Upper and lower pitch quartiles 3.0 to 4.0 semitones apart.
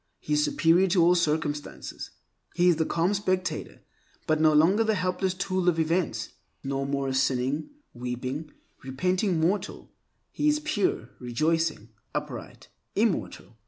No: average, 4.4 semitones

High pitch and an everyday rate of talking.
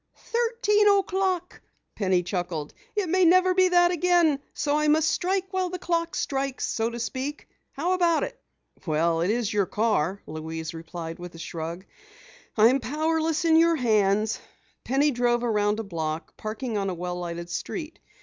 Yes: high, 245 Hz; average, 160 wpm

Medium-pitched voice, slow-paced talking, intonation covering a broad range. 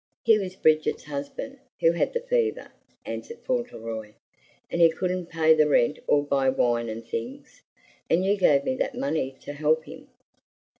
No: medium, 160 Hz; average, 165 wpm; wide, 6.1 semitones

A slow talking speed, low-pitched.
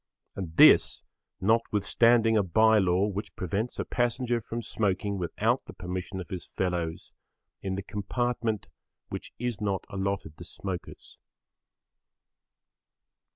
Yes: slow, 120 wpm; low, 100 Hz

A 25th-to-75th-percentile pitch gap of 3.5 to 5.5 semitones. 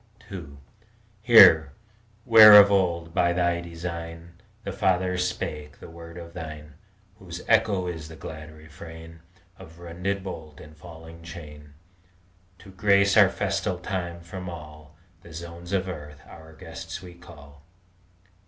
No: narrow, 2.4 semitones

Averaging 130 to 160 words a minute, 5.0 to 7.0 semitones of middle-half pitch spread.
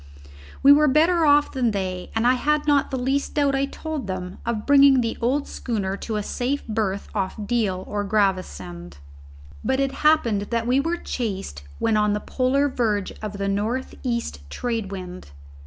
No: average, 180 wpm; wide, 5.6 semitones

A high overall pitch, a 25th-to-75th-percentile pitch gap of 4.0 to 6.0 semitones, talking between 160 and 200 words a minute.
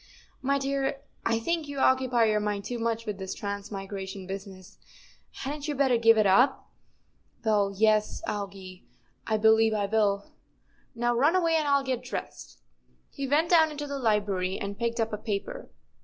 Yes: high, 225 Hz; average, 5.1 semitones; average, 175 wpm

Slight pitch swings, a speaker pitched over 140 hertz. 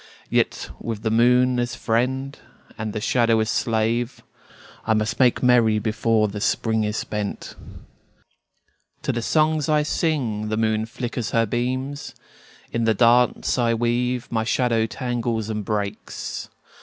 No: narrow, 2.1 semitones; low, 115 Hz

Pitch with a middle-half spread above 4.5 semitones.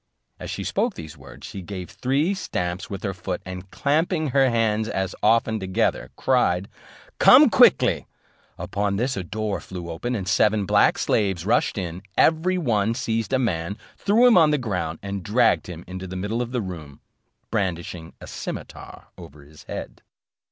Yes: average, 5.2 semitones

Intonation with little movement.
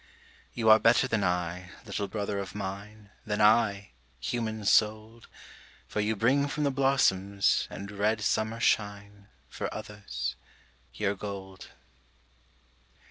Yes: narrow, 2.0 semitones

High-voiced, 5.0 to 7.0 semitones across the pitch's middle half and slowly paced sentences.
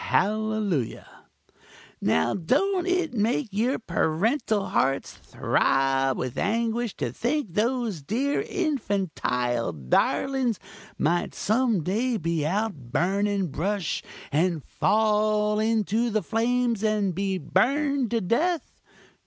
Yes: high, 215 Hz; wide, 5.5 semitones; slow, 105 wpm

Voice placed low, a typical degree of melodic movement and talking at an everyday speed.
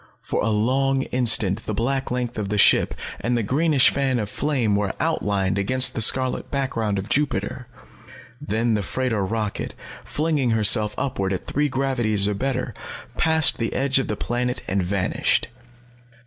Yes: low, 120 Hz; average, 4.2 semitones; average, 160 wpm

